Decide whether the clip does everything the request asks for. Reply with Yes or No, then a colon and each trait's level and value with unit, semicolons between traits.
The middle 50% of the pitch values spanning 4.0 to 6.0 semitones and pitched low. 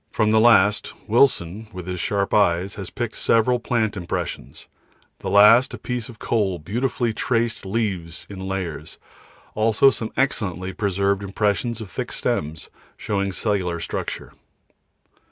No: average, 3.5 semitones; low, 105 Hz